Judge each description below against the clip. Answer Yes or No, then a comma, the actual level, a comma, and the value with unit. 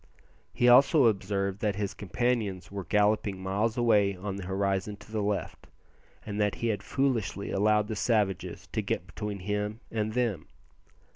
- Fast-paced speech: No, average, 160 wpm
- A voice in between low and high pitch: No, low, 105 Hz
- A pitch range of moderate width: No, narrow, 2.0 semitones